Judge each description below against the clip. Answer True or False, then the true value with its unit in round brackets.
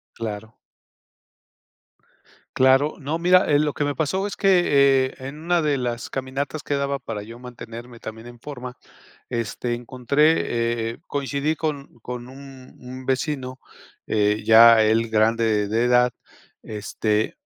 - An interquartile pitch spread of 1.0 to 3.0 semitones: False (3.6 semitones)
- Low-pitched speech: True (125 Hz)